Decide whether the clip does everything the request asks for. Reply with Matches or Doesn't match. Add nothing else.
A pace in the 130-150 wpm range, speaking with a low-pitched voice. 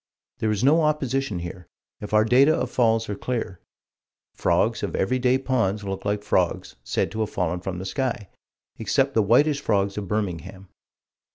Doesn't match